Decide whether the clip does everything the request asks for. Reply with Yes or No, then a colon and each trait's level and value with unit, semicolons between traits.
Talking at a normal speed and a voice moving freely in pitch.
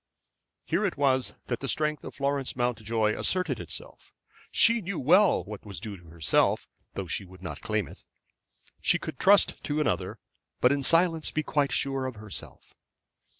Yes: average, 170 wpm; wide, 6.3 semitones